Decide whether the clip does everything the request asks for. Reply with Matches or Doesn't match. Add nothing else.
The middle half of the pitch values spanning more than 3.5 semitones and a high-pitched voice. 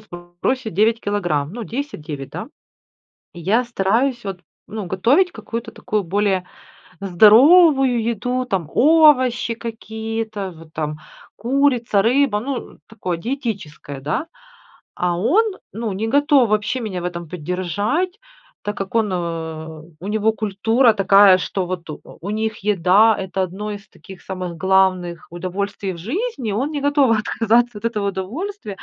Matches